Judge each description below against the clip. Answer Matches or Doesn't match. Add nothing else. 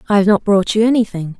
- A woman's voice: Matches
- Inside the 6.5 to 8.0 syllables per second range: Matches